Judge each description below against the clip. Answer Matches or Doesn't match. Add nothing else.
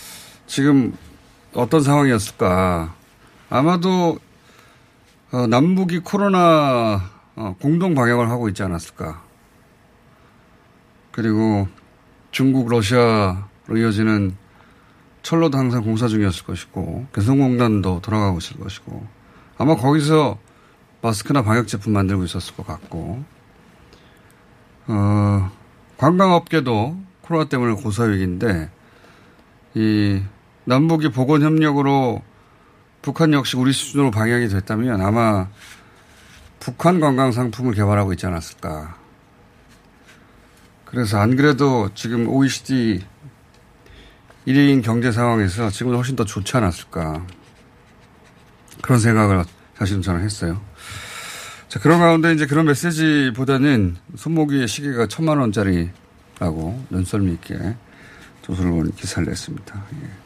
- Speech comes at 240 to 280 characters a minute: Matches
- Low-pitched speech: Matches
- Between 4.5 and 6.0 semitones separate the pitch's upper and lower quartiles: Matches